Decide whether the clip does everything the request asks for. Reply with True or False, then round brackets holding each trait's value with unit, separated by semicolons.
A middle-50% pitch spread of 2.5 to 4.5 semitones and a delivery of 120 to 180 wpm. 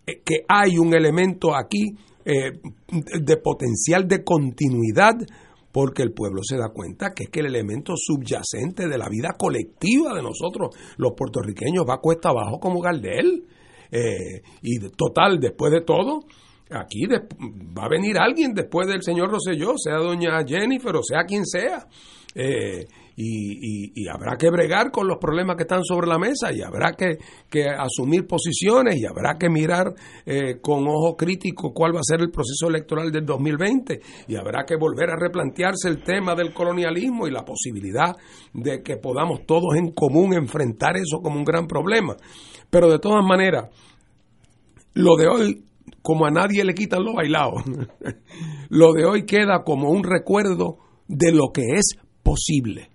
True (4.0 semitones; 170 wpm)